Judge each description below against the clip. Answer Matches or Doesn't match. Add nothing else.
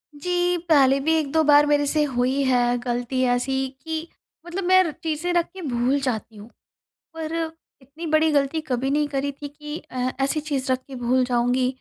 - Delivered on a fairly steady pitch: Doesn't match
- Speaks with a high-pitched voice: Matches